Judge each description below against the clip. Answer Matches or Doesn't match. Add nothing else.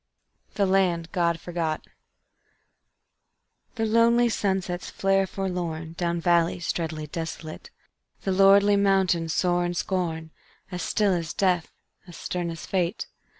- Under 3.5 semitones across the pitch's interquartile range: Matches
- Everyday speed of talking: Doesn't match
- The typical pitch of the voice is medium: Matches